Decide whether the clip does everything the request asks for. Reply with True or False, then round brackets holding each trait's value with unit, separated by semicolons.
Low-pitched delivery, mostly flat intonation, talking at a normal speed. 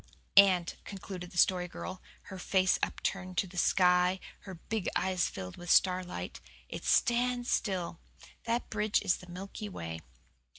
False (185 Hz; 1.8 semitones; 155 wpm)